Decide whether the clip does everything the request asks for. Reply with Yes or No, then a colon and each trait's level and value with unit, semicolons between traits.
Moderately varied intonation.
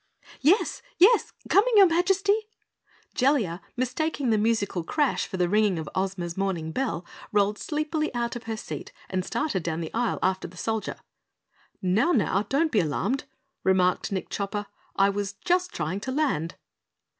No: wide, 7.8 semitones